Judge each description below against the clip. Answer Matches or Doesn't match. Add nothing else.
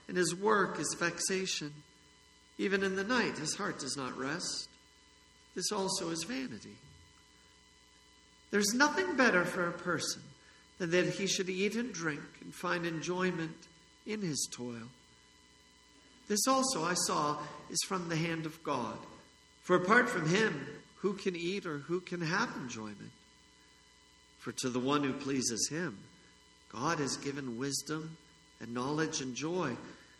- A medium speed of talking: Matches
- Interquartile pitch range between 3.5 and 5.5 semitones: Matches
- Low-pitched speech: Doesn't match